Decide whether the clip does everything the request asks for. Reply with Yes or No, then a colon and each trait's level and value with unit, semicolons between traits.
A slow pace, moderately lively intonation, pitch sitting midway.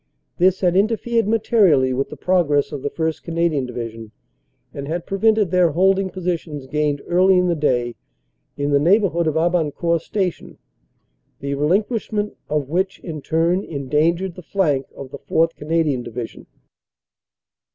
No: average, 150 wpm; average, 4.6 semitones; medium, 165 Hz